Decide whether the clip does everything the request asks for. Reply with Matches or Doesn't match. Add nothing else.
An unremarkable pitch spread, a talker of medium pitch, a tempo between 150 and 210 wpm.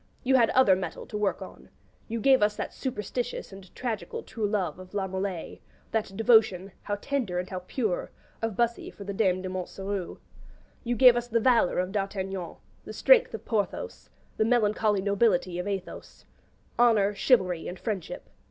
Doesn't match